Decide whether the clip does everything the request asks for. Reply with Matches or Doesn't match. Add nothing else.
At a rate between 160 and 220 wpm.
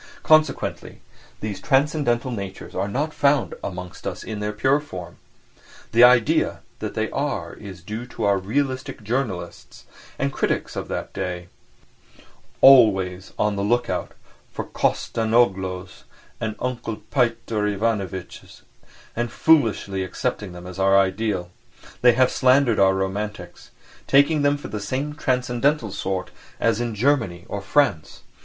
Doesn't match